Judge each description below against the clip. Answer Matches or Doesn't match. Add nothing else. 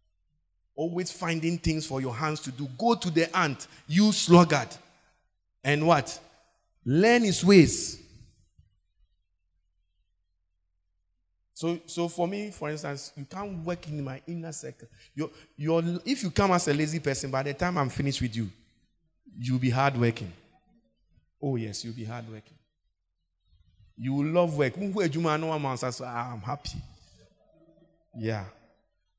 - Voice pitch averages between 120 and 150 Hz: Matches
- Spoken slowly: Matches